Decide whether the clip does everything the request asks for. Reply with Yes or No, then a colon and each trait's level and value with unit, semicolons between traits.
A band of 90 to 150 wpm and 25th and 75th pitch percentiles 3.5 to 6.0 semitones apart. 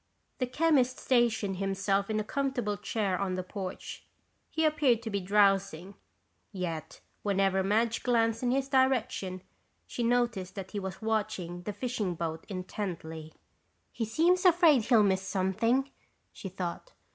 Yes: average, 145 wpm; average, 4.4 semitones